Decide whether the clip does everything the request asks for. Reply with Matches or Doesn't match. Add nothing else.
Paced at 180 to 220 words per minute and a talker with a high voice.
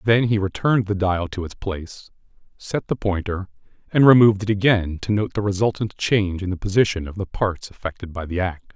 Doesn't match